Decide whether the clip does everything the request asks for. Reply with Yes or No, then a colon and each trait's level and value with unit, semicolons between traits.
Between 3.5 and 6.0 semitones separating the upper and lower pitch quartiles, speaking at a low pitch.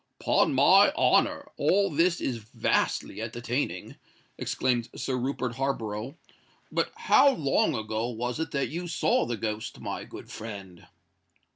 Yes: average, 4.2 semitones; low, 120 Hz